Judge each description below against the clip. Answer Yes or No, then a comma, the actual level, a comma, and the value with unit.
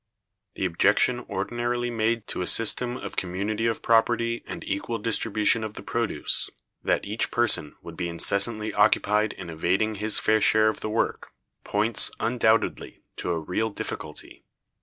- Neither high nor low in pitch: No, low, 110 Hz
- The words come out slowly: No, average, 155 wpm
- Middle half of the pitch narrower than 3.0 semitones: Yes, narrow, 2.6 semitones